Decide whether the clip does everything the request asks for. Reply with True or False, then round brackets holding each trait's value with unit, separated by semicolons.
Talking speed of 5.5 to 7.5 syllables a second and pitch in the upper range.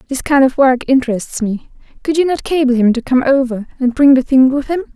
True (5.7 syllables/s; 265 Hz)